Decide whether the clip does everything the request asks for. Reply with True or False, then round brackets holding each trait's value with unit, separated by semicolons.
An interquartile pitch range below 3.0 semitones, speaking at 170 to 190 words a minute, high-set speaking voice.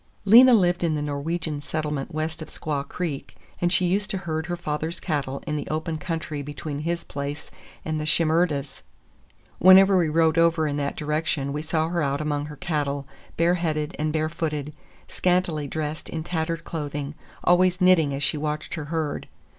False (2.5 semitones; 175 wpm; 155 Hz)